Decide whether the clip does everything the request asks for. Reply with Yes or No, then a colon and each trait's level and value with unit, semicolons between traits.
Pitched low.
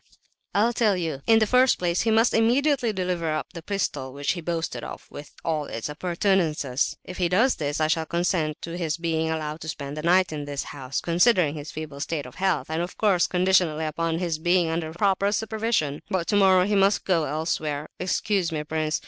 No: medium, 170 Hz